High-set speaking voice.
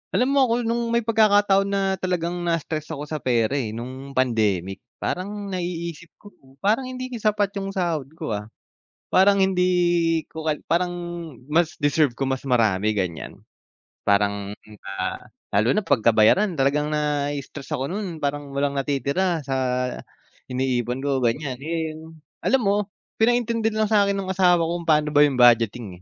No: medium, 155 Hz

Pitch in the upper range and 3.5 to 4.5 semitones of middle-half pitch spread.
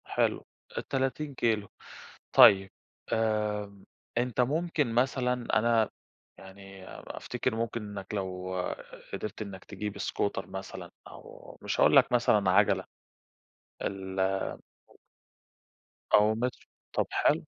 No: low, 105 Hz; average, 3.8 semitones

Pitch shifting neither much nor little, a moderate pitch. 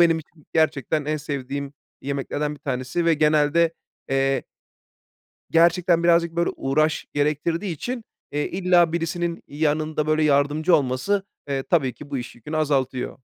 Yes: average, 3.0 semitones; medium, 155 Hz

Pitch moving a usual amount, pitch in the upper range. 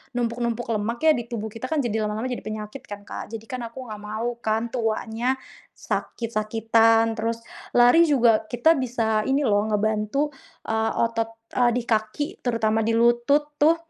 No: narrow, 2.0 semitones; high, 230 Hz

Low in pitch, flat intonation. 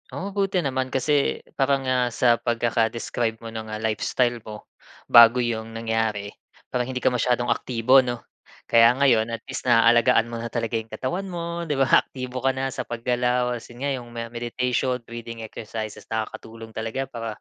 Yes: low, 120 Hz; narrow, 2.3 semitones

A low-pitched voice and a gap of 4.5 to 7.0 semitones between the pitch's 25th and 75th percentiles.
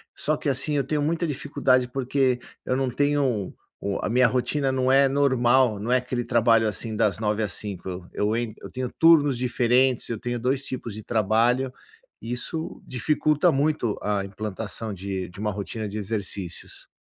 No: low, 120 Hz; average, 4.0 semitones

